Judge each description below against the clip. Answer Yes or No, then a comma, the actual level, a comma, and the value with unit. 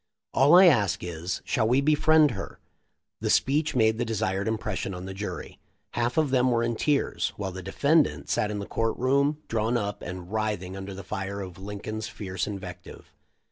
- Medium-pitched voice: No, low, 110 Hz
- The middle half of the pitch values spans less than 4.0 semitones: No, average, 5.1 semitones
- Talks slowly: No, average, 195 wpm